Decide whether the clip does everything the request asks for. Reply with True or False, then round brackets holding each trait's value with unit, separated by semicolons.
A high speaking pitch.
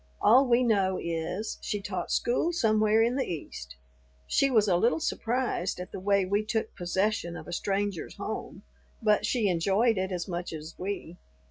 True (200 Hz)